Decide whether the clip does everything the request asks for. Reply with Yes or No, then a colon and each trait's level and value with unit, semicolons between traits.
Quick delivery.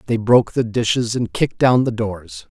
Yes: fast, 210 wpm